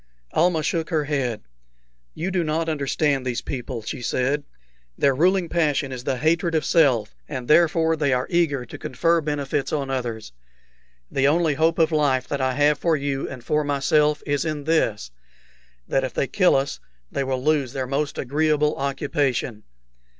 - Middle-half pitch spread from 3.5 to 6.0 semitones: No, average, 3.1 semitones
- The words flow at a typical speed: Yes, average, 170 wpm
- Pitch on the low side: No, medium, 145 Hz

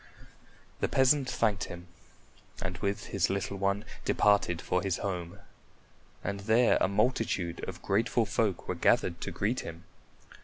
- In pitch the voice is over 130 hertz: No, low, 100 Hz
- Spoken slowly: No, average, 145 wpm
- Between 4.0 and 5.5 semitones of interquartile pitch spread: No, average, 3.5 semitones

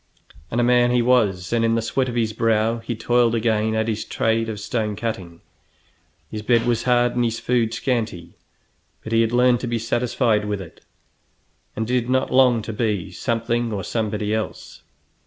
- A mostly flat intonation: Yes, narrow, 2.0 semitones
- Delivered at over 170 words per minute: Yes, average, 190 wpm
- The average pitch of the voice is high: No, low, 115 Hz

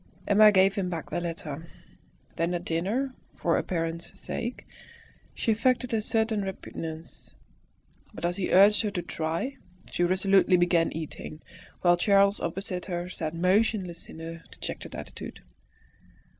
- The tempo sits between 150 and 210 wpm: No, average, 140 wpm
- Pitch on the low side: No, medium, 180 Hz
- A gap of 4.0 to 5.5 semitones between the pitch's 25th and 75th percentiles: No, average, 3.5 semitones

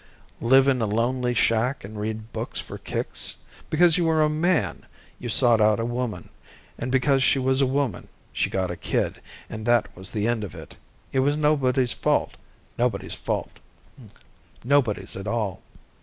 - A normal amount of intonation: Yes, average, 3.9 semitones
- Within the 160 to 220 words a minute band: Yes, average, 165 wpm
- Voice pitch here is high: No, low, 125 Hz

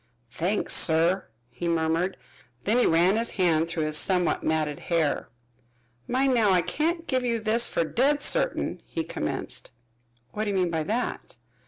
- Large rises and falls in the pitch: Yes, wide, 6.1 semitones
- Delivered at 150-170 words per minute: Yes, average, 165 wpm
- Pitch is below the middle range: No, medium, 185 Hz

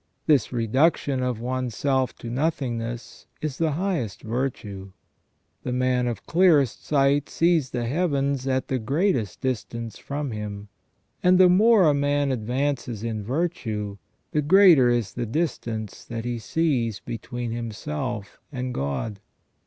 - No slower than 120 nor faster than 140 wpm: Yes, slow, 135 wpm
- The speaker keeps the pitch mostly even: No, average, 4.2 semitones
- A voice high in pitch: No, low, 130 Hz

